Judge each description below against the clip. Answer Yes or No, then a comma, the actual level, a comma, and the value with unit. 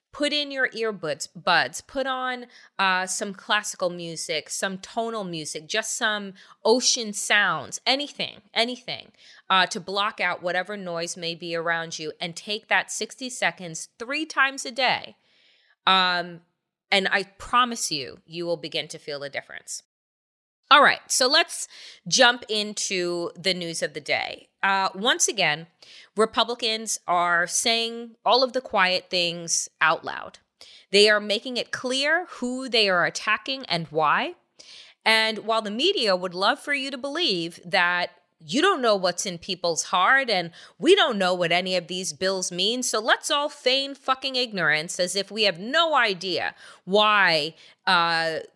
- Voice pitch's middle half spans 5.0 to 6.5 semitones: Yes, wide, 5.6 semitones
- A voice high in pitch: Yes, high, 200 Hz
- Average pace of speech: Yes, average, 160 wpm